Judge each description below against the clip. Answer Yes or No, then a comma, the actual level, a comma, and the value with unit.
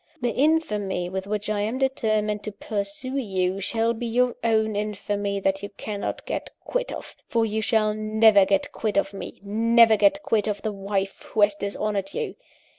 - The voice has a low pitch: No, high, 210 Hz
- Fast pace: No, average, 185 wpm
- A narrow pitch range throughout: Yes, narrow, 2.2 semitones